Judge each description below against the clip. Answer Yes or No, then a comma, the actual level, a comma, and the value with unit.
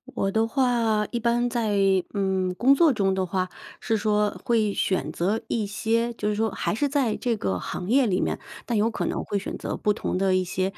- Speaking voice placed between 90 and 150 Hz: No, high, 215 Hz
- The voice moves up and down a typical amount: Yes, average, 3.5 semitones